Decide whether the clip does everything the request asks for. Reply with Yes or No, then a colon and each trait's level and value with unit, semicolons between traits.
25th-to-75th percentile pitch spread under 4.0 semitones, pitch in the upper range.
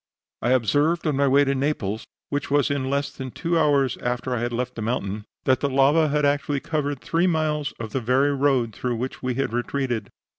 No: average, 2.8 semitones; low, 135 Hz